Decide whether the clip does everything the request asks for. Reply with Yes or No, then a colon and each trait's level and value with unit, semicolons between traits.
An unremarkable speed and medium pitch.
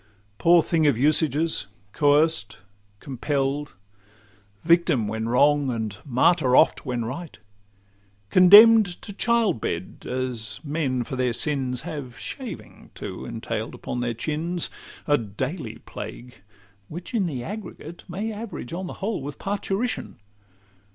No: slow, 125 wpm; medium, 145 Hz